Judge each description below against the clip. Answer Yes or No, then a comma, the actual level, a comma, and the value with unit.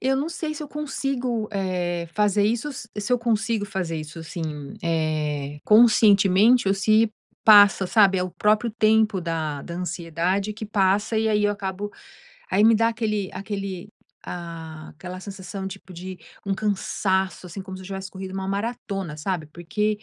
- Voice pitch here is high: Yes, high, 195 Hz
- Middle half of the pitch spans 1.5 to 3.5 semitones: Yes, average, 3.1 semitones